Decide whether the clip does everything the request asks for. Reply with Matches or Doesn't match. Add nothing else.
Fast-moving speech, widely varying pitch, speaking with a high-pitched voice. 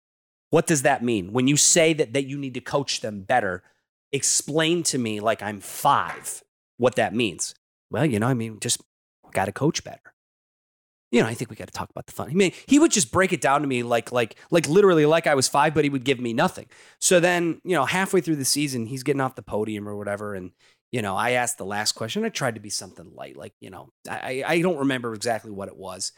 Doesn't match